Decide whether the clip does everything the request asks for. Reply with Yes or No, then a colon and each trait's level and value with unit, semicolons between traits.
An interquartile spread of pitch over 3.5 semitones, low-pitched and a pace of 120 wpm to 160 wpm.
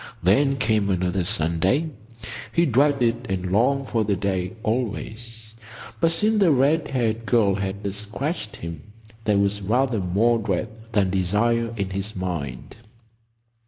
Yes: average, 4.4 semitones; low, 110 Hz; slow, 135 wpm